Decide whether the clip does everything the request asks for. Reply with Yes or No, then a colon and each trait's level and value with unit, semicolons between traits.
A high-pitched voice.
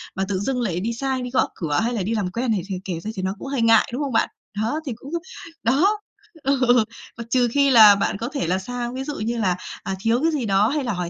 Yes: high, 235 Hz